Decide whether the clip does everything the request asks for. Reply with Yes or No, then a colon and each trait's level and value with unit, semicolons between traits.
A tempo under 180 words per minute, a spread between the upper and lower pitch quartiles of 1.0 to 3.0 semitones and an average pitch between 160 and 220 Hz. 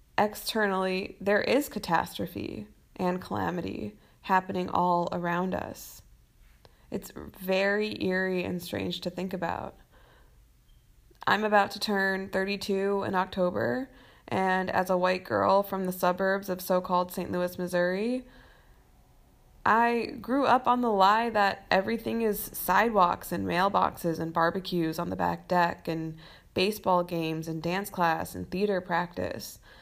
Yes: slow, 135 wpm; narrow, 2.5 semitones; medium, 185 Hz